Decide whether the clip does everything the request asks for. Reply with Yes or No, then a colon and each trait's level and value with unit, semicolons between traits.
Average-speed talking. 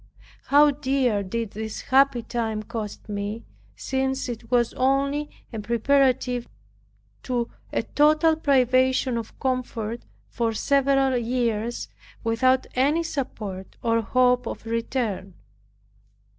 No: slow, 110 wpm